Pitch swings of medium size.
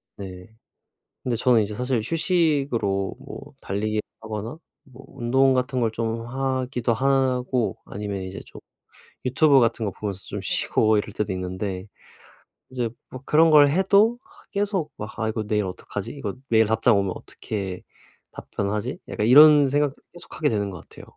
Yes: average, 4.6 semitones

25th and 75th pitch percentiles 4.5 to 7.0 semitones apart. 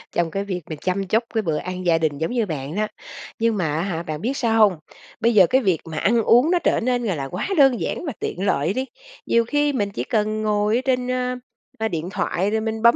Yes: average, 5.1 semitones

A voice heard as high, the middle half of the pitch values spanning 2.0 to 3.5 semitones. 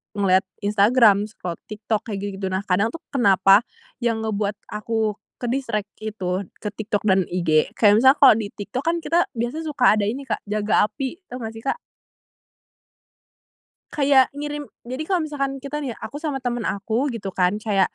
No: high, 220 Hz; average, 4.8 semitones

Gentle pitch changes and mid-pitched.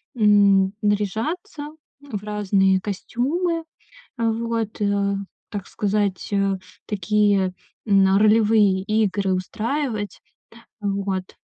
No: narrow, 2.2 semitones; high, 205 Hz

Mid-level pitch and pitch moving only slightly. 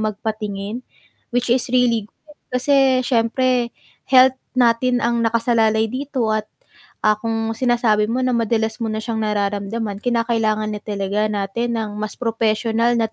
No: high, 230 Hz; narrow, 2.1 semitones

